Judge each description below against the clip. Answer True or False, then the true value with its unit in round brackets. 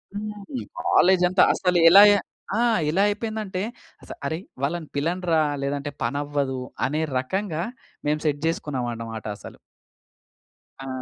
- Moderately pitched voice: True (165 Hz)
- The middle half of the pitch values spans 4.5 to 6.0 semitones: True (5.3 semitones)